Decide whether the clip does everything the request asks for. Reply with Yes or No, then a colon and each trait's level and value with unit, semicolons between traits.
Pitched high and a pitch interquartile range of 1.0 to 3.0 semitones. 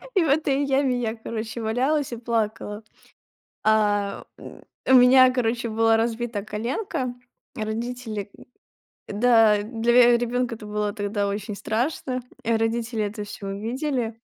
Yes: high, 230 Hz; narrow, 2.6 semitones